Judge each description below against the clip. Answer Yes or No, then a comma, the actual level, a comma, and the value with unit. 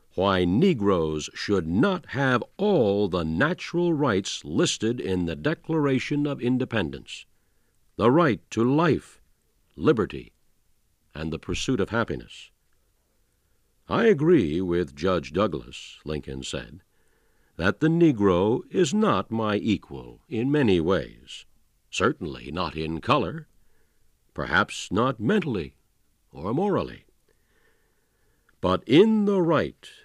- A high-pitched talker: No, low, 110 Hz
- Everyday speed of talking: No, slow, 110 wpm